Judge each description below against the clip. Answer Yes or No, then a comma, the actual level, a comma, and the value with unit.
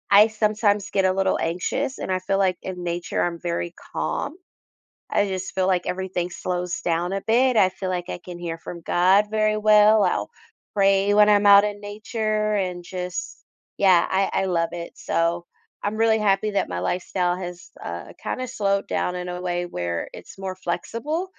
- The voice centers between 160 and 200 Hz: Yes, high, 190 Hz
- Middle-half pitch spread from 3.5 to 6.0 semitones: No, average, 2.8 semitones